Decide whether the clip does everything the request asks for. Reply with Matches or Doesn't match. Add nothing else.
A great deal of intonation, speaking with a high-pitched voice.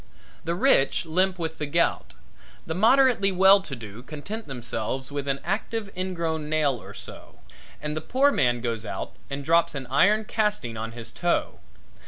Doesn't match